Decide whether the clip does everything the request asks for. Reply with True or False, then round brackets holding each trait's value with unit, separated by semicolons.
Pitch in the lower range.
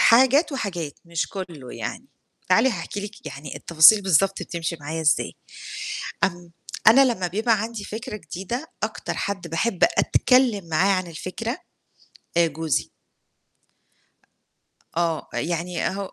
False (185 Hz)